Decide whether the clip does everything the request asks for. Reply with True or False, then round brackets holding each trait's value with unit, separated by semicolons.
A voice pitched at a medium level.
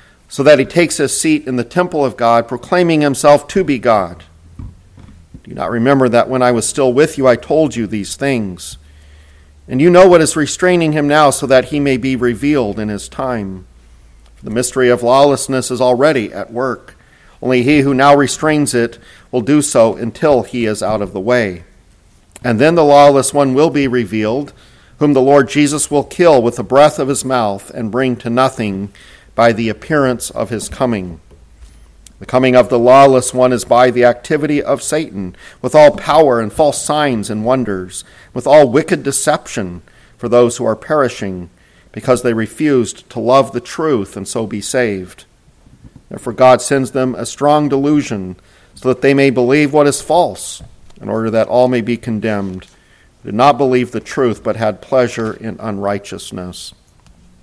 False (125 Hz)